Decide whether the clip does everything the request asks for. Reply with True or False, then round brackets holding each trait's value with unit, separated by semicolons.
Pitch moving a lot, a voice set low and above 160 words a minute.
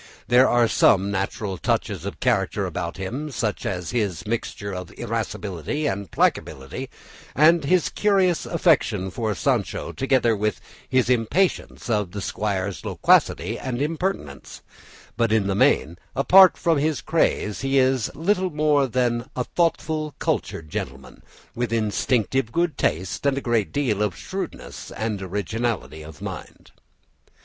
False (6.3 semitones; 115 Hz; 140 wpm)